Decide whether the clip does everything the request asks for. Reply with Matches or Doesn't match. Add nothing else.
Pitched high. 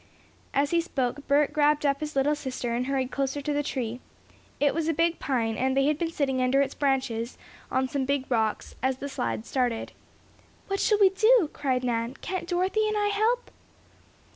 Matches